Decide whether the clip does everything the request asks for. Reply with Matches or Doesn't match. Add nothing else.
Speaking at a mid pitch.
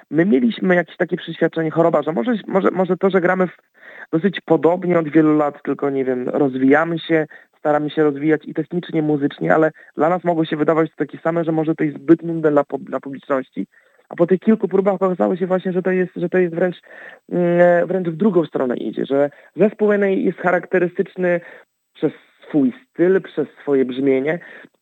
Matches